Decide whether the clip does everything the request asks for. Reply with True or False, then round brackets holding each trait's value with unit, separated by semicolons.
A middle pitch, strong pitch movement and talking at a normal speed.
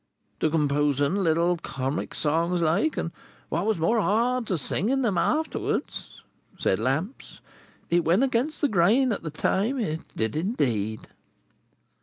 False (175 Hz; 6.9 semitones; 130 wpm)